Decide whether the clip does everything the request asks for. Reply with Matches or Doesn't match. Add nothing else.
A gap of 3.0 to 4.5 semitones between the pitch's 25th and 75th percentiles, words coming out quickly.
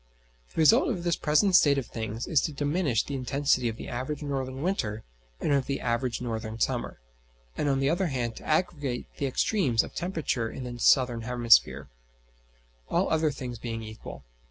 Doesn't match